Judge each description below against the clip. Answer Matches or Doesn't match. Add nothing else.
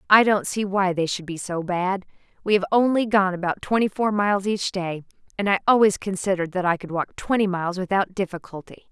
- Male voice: Doesn't match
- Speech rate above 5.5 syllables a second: Matches